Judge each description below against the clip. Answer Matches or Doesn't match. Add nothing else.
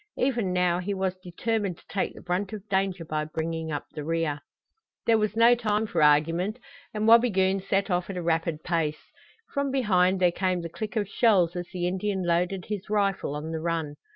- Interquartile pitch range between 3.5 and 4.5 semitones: Matches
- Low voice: Doesn't match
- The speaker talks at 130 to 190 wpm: Doesn't match